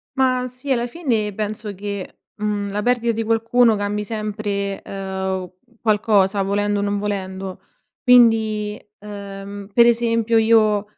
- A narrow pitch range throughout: Yes, narrow, 2.3 semitones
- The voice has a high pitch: Yes, high, 210 Hz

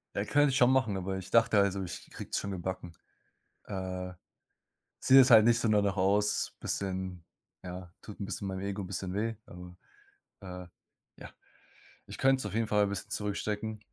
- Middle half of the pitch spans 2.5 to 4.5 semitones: Yes, average, 2.8 semitones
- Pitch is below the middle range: Yes, low, 100 Hz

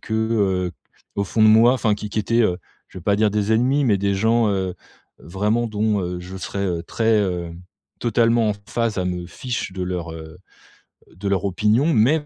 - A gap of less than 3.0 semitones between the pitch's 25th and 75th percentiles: No, average, 3.5 semitones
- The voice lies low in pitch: Yes, low, 105 Hz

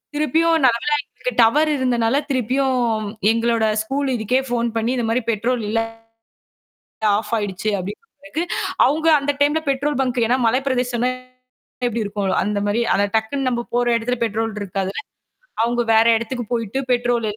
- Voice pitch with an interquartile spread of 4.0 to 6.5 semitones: No, average, 3.2 semitones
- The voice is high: Yes, high, 240 Hz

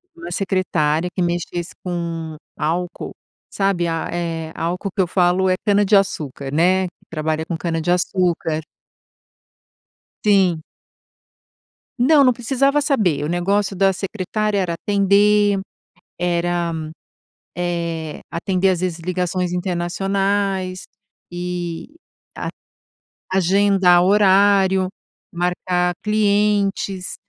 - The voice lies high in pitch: No, medium, 180 Hz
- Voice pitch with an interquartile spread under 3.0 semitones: Yes, narrow, 2.4 semitones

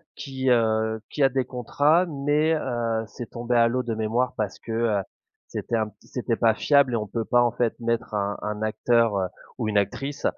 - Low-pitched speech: Yes, low, 115 Hz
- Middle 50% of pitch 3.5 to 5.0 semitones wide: No, average, 2.7 semitones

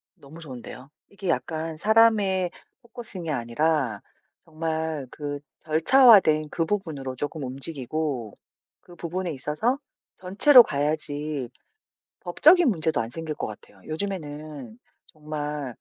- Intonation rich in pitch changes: No, average, 4.2 semitones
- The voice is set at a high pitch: No, medium, 155 Hz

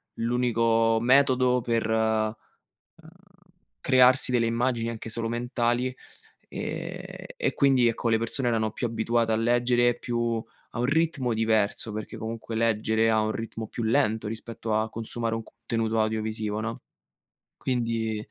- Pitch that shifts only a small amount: Yes, narrow, 1.5 semitones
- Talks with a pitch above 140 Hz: No, low, 115 Hz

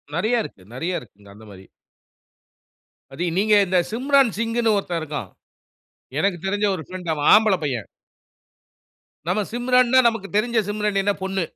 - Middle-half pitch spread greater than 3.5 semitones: Yes, wide, 5.5 semitones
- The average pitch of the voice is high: Yes, high, 195 Hz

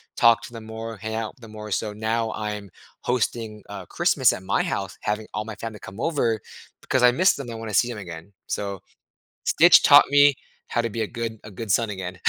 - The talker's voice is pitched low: Yes, low, 110 Hz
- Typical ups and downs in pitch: No, narrow, 1.9 semitones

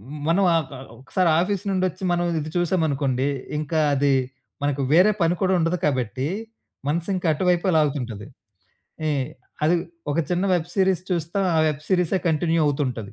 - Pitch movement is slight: No, average, 4.0 semitones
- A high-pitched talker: No, medium, 165 Hz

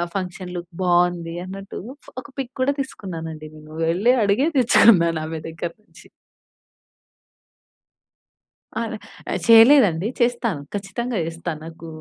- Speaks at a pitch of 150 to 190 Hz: Yes, medium, 185 Hz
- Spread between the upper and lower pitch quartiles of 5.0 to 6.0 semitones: Yes, wide, 5.6 semitones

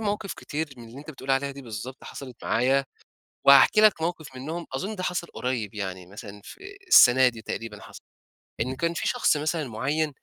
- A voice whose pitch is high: No, low, 135 Hz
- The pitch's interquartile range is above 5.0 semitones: Yes, wide, 5.4 semitones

